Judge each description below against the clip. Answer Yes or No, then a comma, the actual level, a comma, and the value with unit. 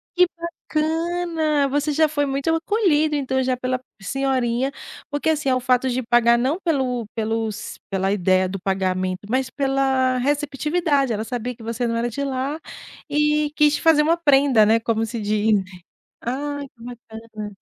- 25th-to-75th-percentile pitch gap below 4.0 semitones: No, average, 4.4 semitones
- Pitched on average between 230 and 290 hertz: Yes, very high, 260 Hz